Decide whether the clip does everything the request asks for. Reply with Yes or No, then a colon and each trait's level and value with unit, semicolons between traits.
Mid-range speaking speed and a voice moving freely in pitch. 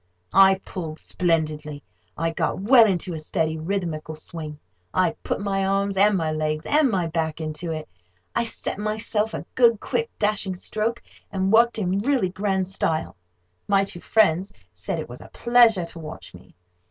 No: average, 170 wpm; average, 4.8 semitones